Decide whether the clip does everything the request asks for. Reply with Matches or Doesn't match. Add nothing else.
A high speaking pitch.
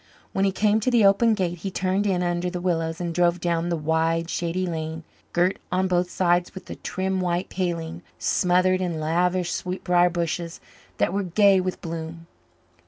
Doesn't match